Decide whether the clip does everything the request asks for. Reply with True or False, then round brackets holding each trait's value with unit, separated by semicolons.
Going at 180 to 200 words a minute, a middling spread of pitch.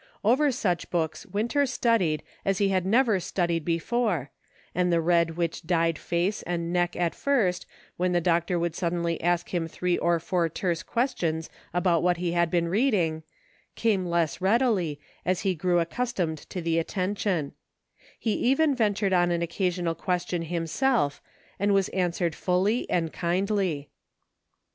False (155 wpm; 3.0 semitones)